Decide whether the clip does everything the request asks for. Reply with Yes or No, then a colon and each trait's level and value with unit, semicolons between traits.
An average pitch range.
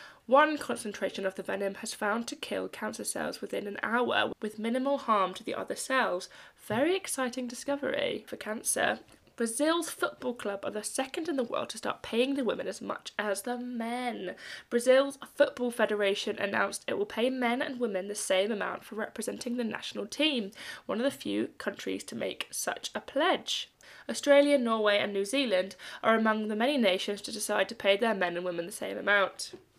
Yes: average, 4.8 semitones